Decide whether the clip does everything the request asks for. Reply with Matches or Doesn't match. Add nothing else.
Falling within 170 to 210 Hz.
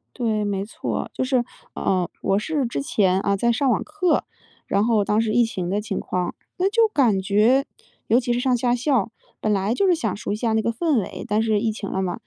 Doesn't match